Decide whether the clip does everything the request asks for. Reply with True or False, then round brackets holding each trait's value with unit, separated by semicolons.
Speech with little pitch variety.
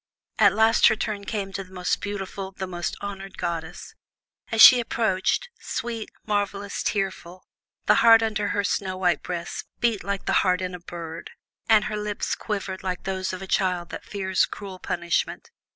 True (2.2 semitones)